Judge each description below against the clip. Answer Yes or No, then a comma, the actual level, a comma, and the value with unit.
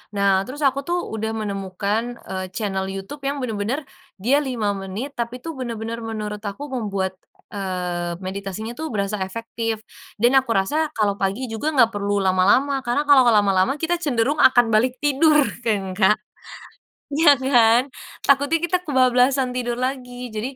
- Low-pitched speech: No, high, 230 Hz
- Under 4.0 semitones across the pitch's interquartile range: No, average, 4.8 semitones